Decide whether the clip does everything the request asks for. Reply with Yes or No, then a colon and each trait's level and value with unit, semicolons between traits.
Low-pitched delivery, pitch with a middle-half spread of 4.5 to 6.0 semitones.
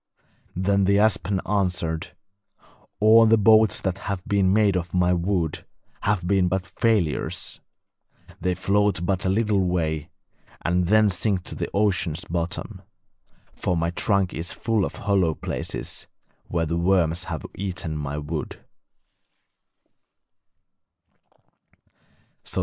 No: very low, 95 Hz; average, 2.9 semitones